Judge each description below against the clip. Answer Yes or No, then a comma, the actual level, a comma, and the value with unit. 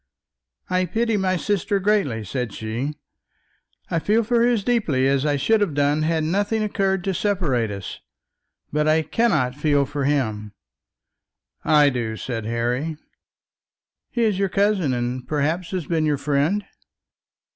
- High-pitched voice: No, medium, 155 Hz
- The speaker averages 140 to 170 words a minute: Yes, average, 150 wpm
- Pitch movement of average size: No, wide, 6.9 semitones